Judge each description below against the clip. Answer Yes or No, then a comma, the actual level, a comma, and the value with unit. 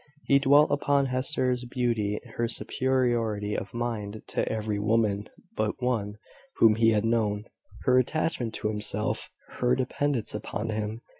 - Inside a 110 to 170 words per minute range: Yes, average, 140 wpm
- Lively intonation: No, average, 3.2 semitones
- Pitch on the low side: Yes, low, 115 Hz